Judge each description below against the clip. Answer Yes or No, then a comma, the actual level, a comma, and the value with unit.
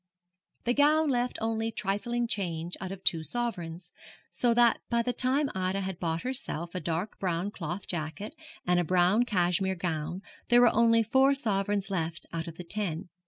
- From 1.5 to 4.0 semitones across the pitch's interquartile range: No, average, 5.2 semitones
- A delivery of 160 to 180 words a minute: Yes, average, 175 wpm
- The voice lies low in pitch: No, high, 195 Hz